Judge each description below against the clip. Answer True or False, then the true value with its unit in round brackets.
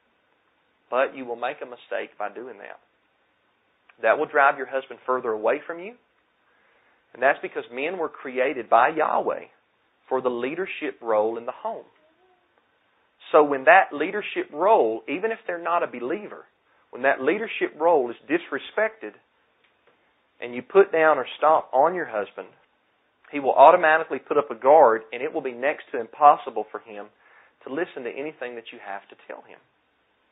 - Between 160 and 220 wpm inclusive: True (170 wpm)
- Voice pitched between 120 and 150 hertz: True (135 Hz)